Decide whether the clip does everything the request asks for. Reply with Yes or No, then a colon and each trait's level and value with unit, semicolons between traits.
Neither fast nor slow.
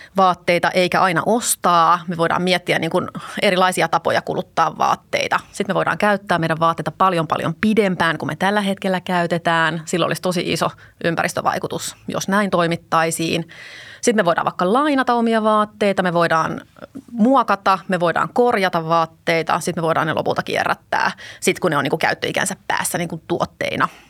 No: fast, 165 wpm